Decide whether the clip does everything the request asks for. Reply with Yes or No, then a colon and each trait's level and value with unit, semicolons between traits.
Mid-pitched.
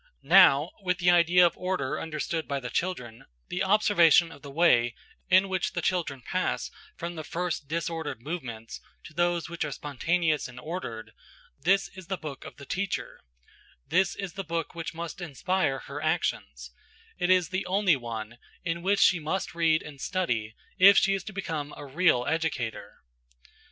Yes: medium, 165 Hz